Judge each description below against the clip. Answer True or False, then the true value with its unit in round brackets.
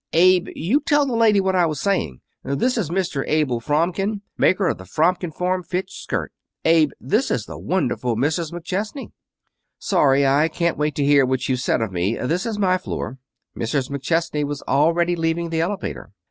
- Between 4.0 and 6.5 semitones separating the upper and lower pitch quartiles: True (4.9 semitones)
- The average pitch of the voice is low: False (165 Hz)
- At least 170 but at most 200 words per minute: True (185 wpm)